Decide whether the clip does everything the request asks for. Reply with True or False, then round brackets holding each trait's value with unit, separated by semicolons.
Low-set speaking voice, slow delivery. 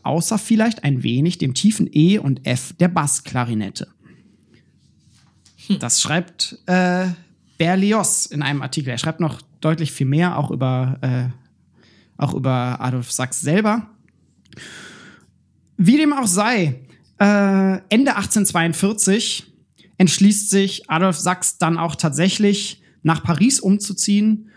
False (180 Hz; 120 wpm)